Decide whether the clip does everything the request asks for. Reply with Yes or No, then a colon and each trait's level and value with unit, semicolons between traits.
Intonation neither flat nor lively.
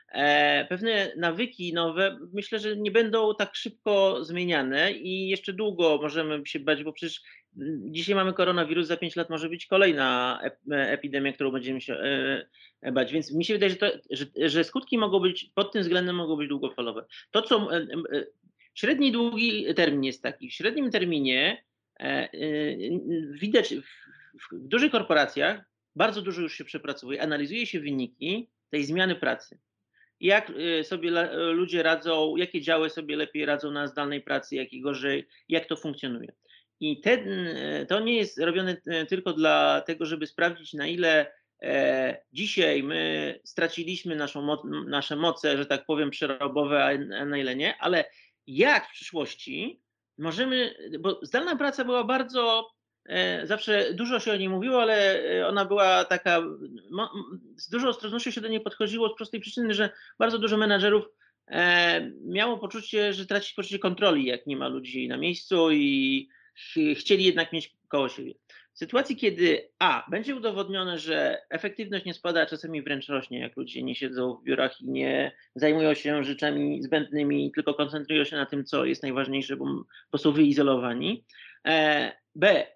No: wide, 6.1 semitones